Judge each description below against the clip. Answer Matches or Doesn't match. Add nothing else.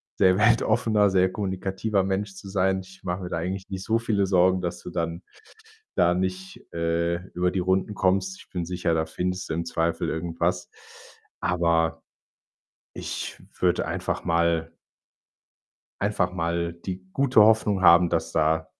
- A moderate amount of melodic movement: Doesn't match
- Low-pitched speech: Matches